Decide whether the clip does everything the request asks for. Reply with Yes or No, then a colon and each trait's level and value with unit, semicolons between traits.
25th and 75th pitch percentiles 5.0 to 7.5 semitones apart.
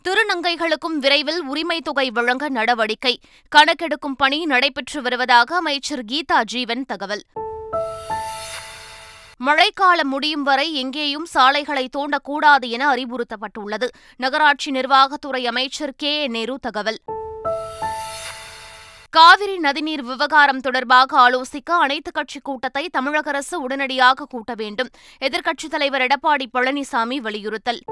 No: average, 3.3 semitones